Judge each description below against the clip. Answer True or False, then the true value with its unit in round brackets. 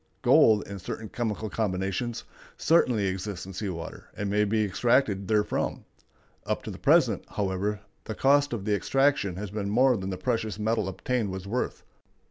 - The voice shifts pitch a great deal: False (3.1 semitones)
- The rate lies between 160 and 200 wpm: True (170 wpm)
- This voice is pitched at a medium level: False (105 Hz)